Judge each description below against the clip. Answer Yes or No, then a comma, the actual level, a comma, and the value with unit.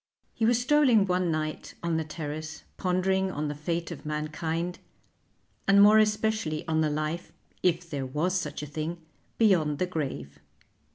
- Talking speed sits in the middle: Yes, average, 160 wpm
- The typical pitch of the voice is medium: Yes, medium, 165 Hz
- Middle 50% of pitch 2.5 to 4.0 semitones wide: Yes, average, 3.7 semitones